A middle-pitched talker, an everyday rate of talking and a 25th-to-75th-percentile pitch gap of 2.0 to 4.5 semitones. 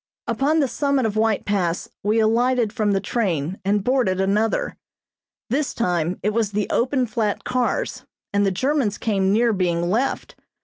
No: high, 215 Hz; average, 165 wpm; average, 4.2 semitones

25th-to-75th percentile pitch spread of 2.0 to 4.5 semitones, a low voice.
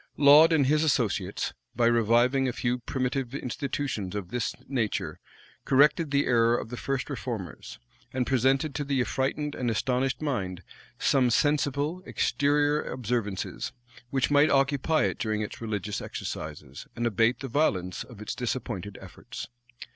Yes: average, 4.1 semitones; low, 125 Hz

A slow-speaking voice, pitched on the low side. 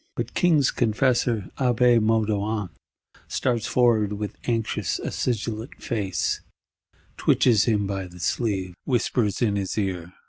Yes: slow, 115 wpm; low, 110 Hz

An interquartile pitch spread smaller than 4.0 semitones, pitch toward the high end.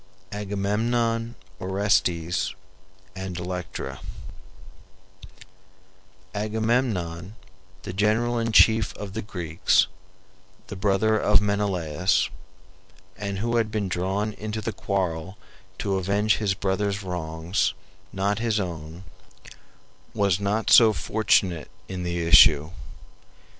No: average, 3.1 semitones; low, 100 Hz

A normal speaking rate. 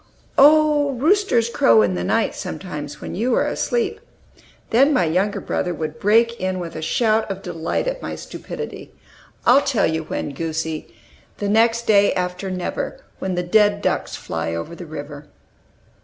Yes: average, 165 wpm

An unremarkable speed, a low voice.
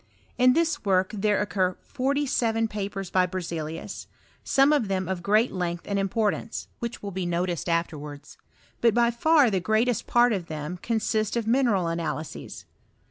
No: average, 165 wpm; high, 200 Hz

